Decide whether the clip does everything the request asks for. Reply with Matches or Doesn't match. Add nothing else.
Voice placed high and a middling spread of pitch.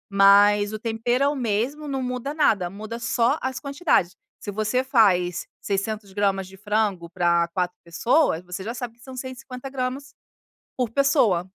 Matches